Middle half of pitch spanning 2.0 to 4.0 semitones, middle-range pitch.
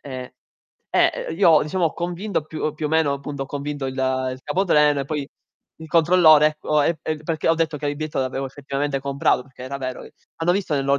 Yes: average, 2.7 semitones; medium, 150 Hz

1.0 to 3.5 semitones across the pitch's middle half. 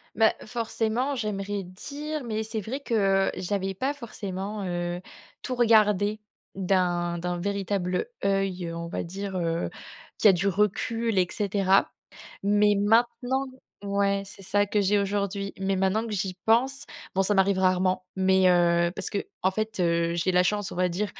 Yes: average, 2.7 semitones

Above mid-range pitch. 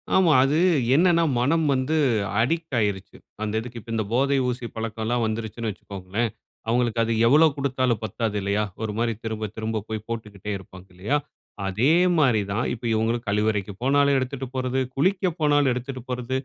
No: low, 120 Hz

